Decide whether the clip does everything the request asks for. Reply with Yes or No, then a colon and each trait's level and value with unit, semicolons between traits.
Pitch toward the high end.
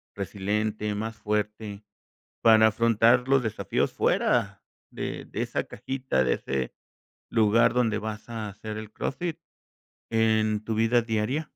No: low, 110 Hz